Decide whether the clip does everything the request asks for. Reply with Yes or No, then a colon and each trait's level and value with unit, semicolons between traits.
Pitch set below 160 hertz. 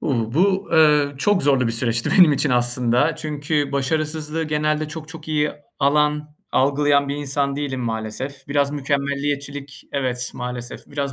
Yes: medium, 140 Hz